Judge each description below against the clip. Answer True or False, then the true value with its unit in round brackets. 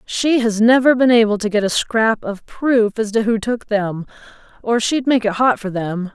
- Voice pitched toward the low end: False (220 Hz)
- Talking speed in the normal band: False (225 wpm)